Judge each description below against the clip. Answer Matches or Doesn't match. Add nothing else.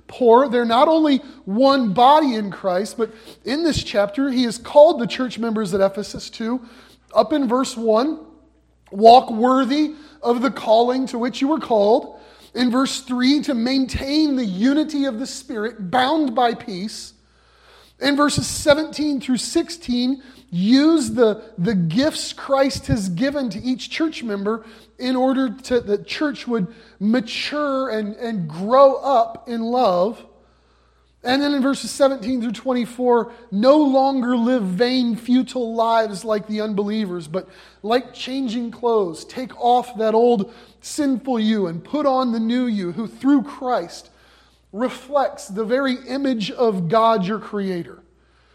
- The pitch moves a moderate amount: Matches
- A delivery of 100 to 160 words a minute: Matches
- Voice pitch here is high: Matches